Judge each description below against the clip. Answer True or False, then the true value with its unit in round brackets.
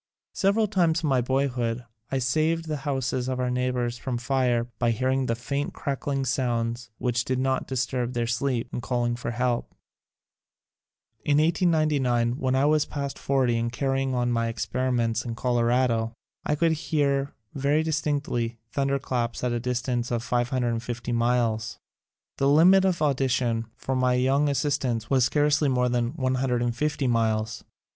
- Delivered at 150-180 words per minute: True (155 wpm)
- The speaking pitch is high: False (125 Hz)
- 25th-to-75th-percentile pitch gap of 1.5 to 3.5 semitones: True (2.7 semitones)